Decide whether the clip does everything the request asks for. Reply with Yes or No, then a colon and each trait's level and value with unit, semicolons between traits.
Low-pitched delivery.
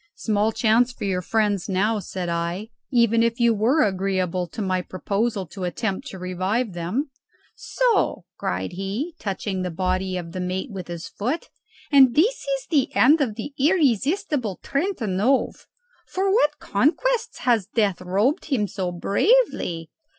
No: high, 210 Hz